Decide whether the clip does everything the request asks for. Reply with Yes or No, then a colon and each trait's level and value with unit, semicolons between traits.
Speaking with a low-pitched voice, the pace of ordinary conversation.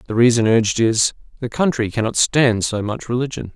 Yes: low, 115 Hz; average, 170 wpm